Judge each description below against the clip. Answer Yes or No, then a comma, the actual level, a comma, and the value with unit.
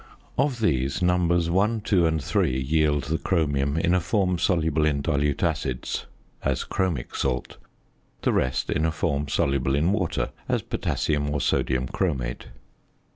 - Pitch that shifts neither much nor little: Yes, average, 4.1 semitones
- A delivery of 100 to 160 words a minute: Yes, average, 150 wpm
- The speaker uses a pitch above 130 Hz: No, very low, 80 Hz